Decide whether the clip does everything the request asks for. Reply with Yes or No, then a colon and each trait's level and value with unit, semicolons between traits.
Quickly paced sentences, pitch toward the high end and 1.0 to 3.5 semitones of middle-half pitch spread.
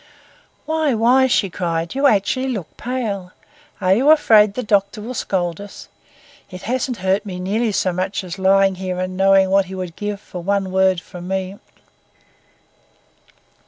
No: average, 160 wpm; high, 195 Hz; average, 3.2 semitones